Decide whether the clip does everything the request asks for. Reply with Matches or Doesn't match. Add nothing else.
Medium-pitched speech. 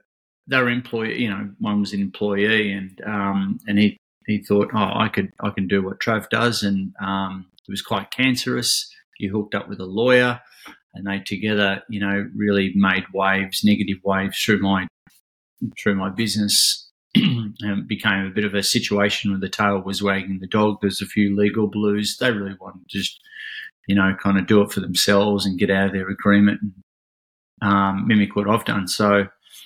Doesn't match